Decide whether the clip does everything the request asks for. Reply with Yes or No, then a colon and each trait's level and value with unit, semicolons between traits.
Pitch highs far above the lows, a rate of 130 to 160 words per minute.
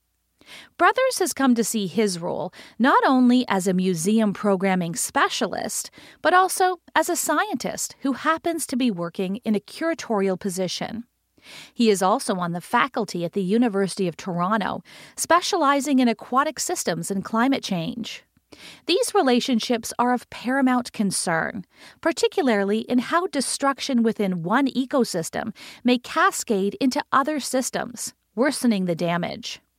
Yes: wide, 6.0 semitones; slow, 135 wpm